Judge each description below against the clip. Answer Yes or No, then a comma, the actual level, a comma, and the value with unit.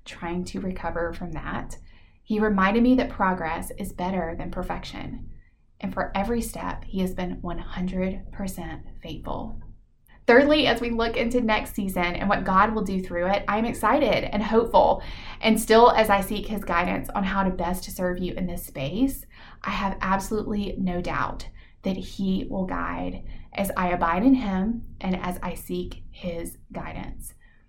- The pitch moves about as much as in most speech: Yes, average, 3.9 semitones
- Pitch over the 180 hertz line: Yes, high, 190 Hz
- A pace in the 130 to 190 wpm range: Yes, average, 170 wpm